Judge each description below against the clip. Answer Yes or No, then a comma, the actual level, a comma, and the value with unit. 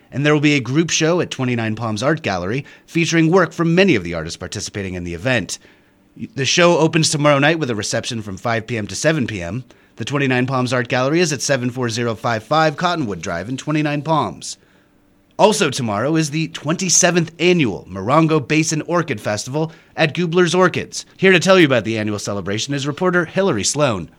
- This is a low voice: No, medium, 145 Hz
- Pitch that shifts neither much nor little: No, wide, 6.1 semitones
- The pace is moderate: Yes, average, 185 wpm